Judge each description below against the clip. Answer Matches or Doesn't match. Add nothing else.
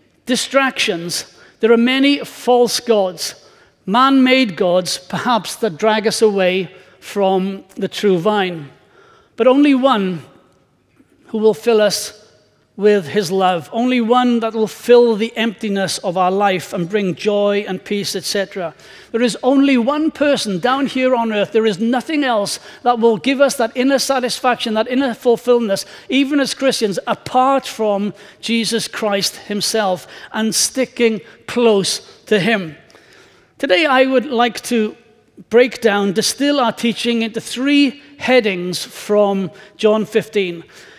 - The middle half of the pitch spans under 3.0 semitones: Doesn't match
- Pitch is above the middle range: Matches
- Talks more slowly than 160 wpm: Matches